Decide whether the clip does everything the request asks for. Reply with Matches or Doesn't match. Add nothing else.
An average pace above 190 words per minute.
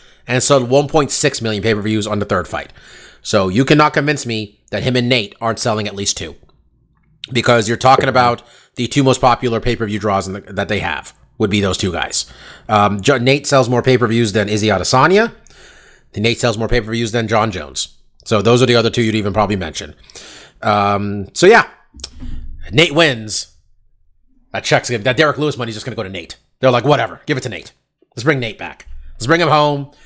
Matches